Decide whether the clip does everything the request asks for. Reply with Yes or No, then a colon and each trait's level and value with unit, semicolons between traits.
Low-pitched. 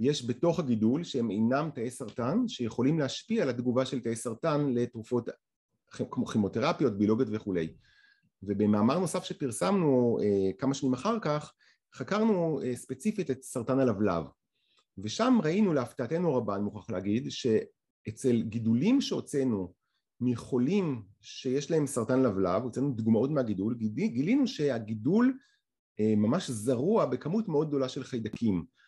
Yes: low, 130 Hz